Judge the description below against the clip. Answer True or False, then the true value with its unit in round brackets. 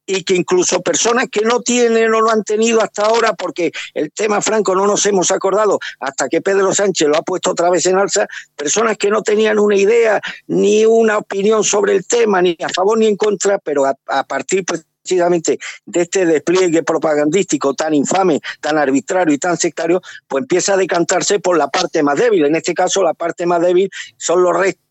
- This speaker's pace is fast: True (200 wpm)